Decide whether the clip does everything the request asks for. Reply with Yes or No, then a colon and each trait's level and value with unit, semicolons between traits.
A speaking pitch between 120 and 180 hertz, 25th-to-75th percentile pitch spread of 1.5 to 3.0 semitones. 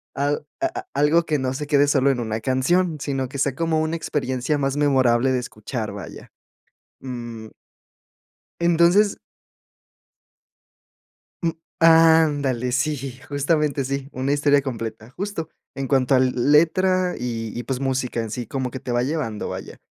No: low, 135 Hz; average, 3.5 semitones